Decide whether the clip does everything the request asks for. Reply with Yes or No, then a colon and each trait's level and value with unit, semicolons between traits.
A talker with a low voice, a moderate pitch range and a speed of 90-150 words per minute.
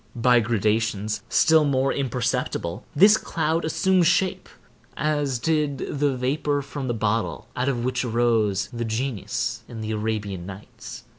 Yes: low, 125 Hz; average, 4.8 semitones; average, 140 wpm